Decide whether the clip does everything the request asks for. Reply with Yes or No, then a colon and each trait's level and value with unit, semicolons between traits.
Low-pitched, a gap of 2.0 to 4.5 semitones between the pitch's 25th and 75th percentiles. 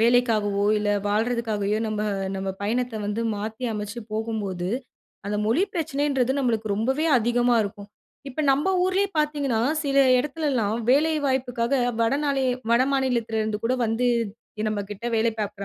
No: high, 230 Hz; average, 4.1 semitones